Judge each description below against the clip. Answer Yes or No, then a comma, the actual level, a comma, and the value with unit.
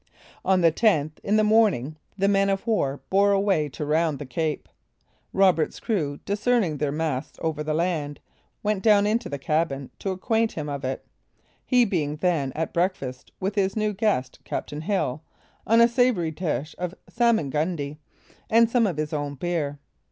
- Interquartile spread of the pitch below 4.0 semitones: No, wide, 5.6 semitones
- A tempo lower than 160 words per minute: No, average, 170 wpm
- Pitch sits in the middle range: Yes, medium, 170 Hz